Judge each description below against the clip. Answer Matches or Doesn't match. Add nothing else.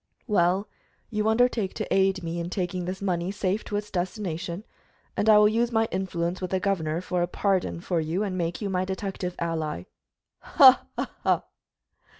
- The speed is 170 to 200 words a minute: Matches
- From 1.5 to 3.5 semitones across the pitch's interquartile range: Matches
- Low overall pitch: Doesn't match